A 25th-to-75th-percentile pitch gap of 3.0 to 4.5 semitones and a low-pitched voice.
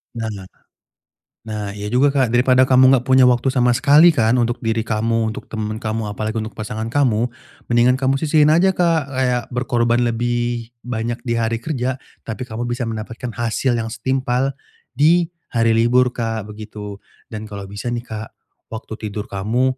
No: narrow, 2.6 semitones; low, 120 Hz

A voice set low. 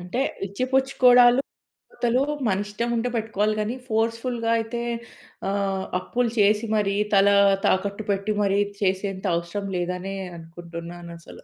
No: high, 205 Hz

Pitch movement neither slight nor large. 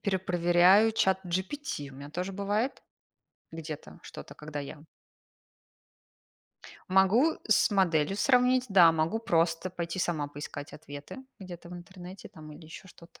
Yes: average, 3.7 semitones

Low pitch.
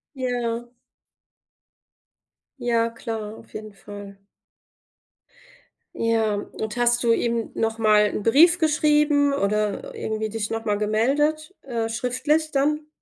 No: high, 230 Hz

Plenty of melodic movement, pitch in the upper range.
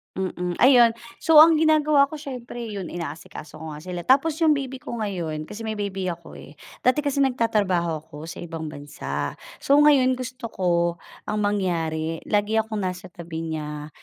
Yes: wide, 7.4 semitones; high, 205 Hz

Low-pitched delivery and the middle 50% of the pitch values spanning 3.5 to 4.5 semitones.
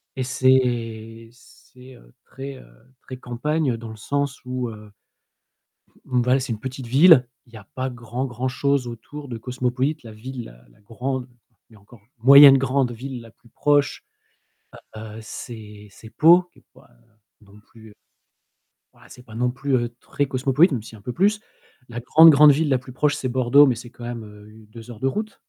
No: low, 125 Hz; average, 3.0 semitones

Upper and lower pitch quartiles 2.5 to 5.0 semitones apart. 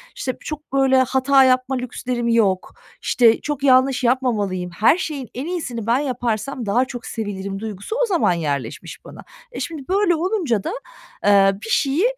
Yes: average, 4.3 semitones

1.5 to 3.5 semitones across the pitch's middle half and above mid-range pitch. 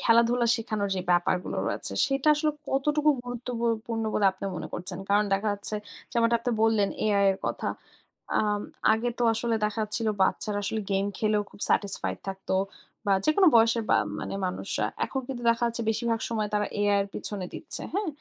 Yes: average, 2.8 semitones; high, 220 Hz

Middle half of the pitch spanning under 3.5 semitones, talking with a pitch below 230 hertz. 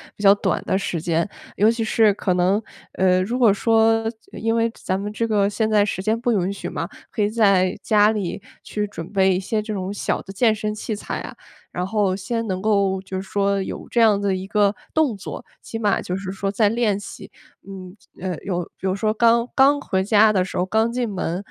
Yes: average, 2.7 semitones; high, 205 Hz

